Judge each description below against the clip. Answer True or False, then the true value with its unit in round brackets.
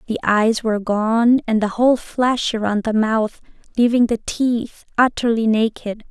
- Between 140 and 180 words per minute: True (155 wpm)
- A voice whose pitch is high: True (225 Hz)